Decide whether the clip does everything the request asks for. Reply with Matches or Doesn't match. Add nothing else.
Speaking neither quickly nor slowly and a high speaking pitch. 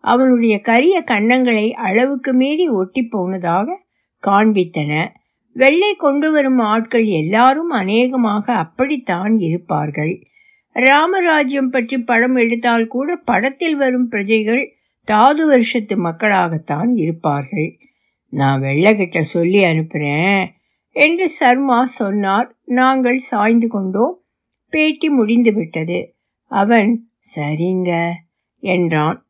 Matches